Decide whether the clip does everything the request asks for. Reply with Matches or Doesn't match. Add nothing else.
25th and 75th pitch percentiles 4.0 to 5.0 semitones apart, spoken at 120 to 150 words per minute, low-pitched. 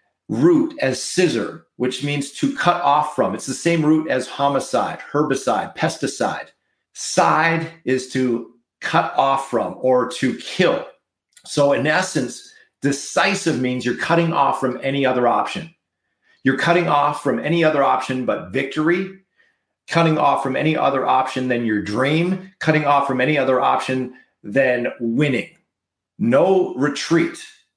Doesn't match